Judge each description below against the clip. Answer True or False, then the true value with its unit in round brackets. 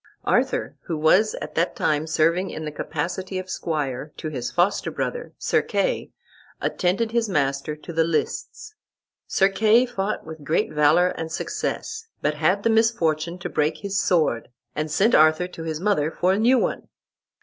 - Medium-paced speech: True (170 wpm)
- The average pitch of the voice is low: False (170 Hz)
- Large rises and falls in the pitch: False (4.8 semitones)